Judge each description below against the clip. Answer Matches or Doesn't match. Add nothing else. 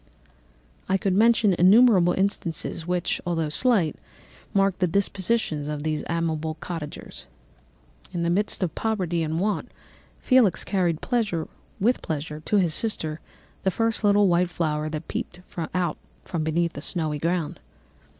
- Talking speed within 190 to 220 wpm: Doesn't match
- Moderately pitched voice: Matches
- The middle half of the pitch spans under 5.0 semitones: Matches